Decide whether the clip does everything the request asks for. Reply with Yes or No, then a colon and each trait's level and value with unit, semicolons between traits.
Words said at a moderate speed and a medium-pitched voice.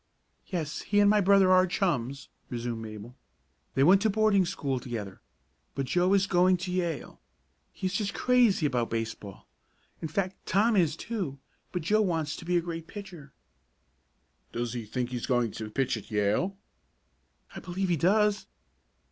Yes: average, 165 wpm; medium, 170 Hz